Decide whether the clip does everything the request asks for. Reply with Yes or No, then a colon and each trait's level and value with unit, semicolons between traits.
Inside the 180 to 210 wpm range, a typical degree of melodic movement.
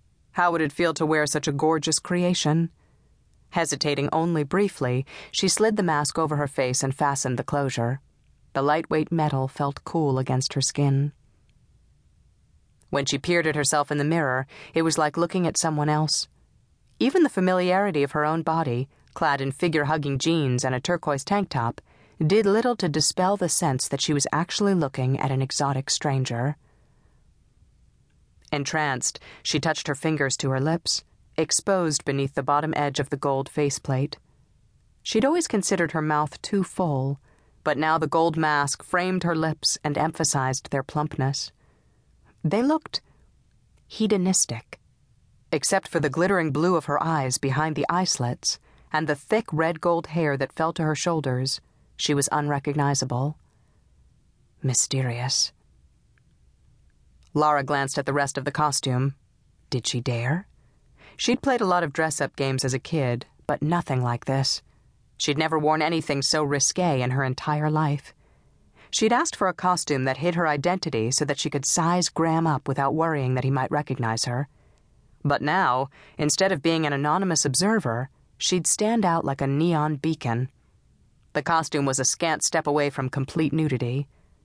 No: average, 165 wpm; average, 3.3 semitones